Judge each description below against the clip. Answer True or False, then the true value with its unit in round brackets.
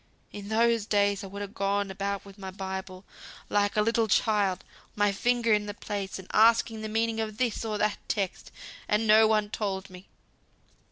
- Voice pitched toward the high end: True (205 Hz)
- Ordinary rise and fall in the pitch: False (1.8 semitones)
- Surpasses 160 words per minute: True (185 wpm)